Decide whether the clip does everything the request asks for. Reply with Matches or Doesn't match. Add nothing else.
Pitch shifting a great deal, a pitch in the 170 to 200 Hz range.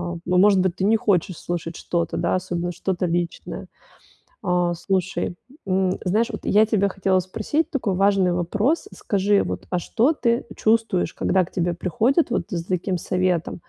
Doesn't match